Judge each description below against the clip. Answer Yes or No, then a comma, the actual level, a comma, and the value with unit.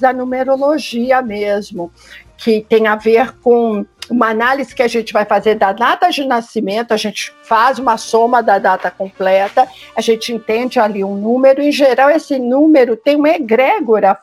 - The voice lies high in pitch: Yes, high, 230 Hz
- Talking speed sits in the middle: Yes, average, 170 wpm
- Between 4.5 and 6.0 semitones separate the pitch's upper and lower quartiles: No, average, 3.5 semitones